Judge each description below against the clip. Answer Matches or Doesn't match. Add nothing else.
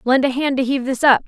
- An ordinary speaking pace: Doesn't match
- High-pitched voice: Matches